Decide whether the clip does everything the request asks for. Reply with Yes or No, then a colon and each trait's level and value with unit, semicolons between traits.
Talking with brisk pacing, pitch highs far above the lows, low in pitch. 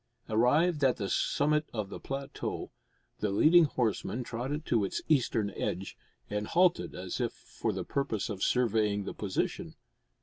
No: average, 155 wpm; wide, 5.7 semitones; low, 120 Hz